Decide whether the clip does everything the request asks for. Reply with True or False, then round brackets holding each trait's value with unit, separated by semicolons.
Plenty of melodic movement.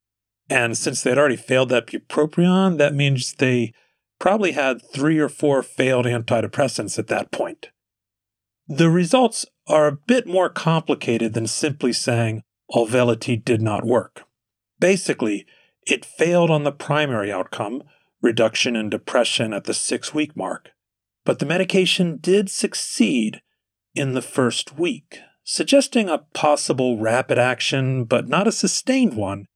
True (6.8 semitones)